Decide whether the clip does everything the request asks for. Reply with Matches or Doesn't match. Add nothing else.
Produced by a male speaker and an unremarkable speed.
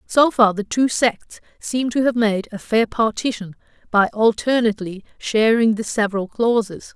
Doesn't match